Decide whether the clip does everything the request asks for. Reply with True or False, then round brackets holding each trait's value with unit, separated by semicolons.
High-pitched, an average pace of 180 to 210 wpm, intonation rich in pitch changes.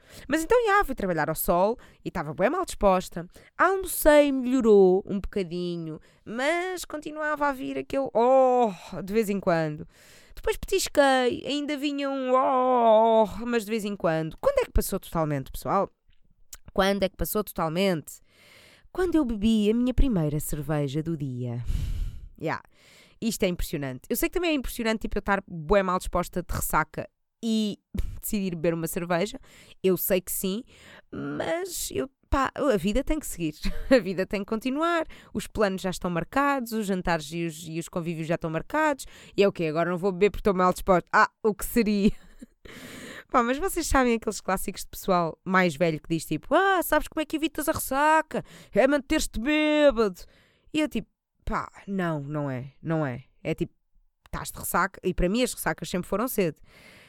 True (205 Hz; 185 wpm; 7.4 semitones)